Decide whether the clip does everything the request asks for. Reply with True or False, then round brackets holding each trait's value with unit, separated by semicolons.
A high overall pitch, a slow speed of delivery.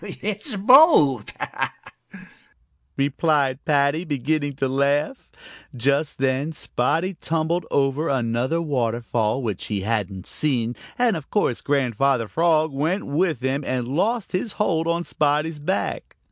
False (145 Hz; 120 wpm)